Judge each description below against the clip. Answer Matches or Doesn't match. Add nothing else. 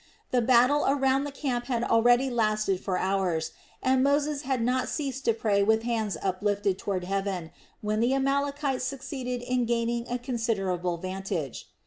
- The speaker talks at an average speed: Matches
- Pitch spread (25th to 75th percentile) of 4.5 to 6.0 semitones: Matches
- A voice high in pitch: Matches